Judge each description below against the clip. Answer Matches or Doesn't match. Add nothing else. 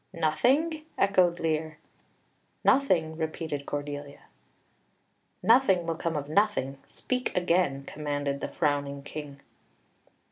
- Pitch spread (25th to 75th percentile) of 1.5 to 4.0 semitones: Doesn't match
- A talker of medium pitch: Matches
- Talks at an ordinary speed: Doesn't match